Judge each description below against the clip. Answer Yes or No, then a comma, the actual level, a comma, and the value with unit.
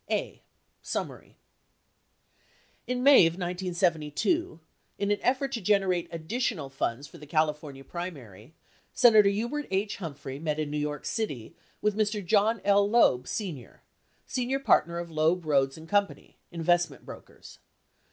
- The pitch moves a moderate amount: No, wide, 5.7 semitones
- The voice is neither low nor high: Yes, medium, 175 Hz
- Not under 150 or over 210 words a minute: No, slow, 135 wpm